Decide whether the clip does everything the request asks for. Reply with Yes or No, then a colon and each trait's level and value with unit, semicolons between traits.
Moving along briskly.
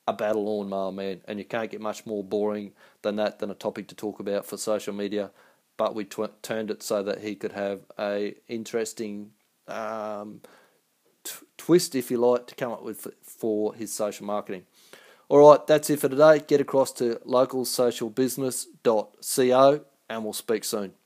No: average, 180 wpm